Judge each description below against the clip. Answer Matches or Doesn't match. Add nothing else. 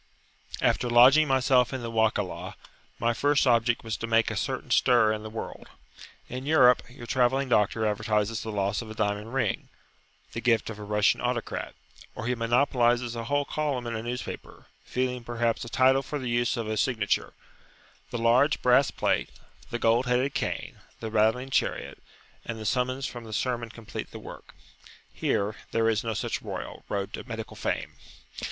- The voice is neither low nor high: Doesn't match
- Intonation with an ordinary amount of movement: Doesn't match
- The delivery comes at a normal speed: Matches